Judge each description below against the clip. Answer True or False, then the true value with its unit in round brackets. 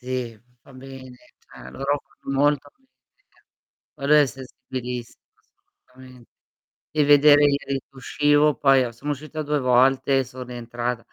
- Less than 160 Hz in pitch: True (135 Hz)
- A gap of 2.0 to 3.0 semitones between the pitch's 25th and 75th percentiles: True (2.5 semitones)